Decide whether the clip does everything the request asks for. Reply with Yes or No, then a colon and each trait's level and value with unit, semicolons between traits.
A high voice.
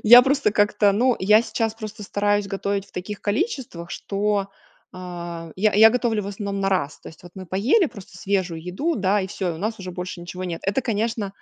Yes: high, 200 Hz